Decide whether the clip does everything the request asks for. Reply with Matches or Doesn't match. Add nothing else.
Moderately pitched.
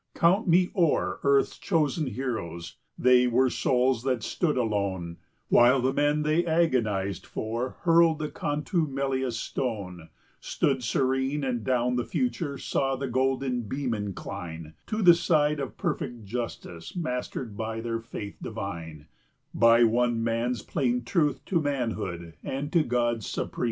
Doesn't match